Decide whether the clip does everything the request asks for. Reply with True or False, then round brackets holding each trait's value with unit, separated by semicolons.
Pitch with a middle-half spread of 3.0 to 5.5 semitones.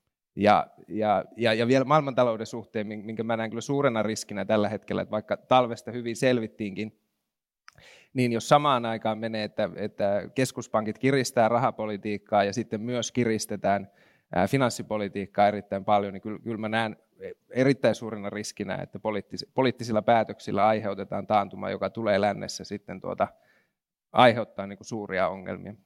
False (2.6 semitones)